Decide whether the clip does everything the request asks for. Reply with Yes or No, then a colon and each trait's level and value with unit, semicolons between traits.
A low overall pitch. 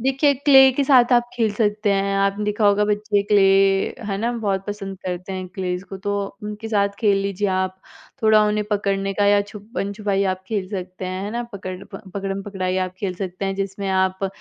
No: high, 200 Hz